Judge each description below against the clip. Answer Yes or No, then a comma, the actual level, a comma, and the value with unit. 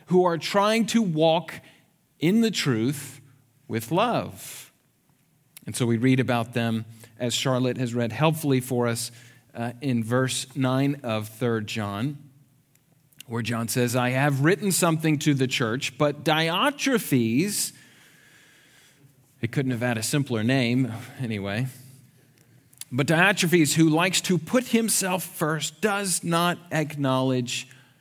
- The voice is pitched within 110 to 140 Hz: Yes, low, 135 Hz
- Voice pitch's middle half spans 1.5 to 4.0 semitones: No, average, 4.5 semitones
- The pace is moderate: No, slow, 130 wpm